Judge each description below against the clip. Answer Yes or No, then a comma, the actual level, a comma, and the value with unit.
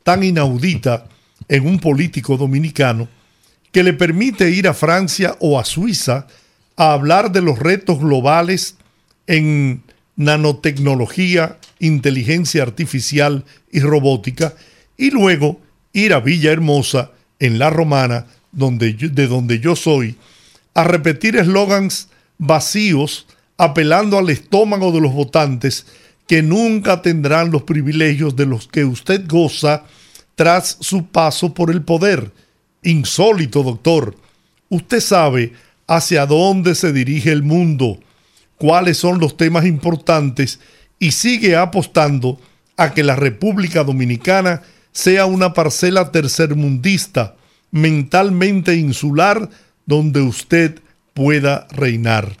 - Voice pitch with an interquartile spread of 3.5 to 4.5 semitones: Yes, average, 4.1 semitones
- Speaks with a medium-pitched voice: Yes, medium, 160 Hz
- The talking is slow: Yes, slow, 115 wpm